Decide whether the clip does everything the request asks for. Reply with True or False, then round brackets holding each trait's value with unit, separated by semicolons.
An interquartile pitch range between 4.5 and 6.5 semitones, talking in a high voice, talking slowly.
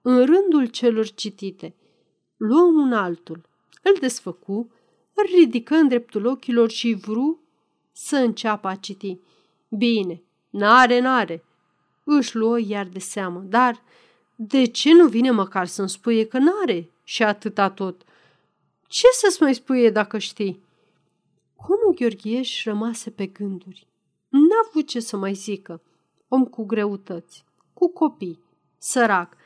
False (4.8 semitones; 225 Hz; 130 wpm)